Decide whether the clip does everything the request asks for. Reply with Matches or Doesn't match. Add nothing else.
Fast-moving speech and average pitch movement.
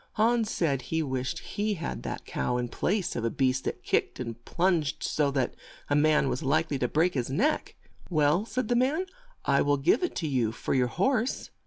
Doesn't match